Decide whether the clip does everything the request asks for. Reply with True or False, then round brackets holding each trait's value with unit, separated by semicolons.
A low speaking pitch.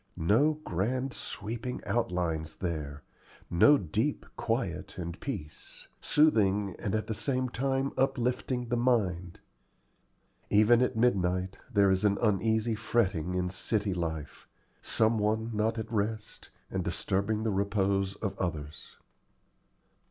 True (105 Hz)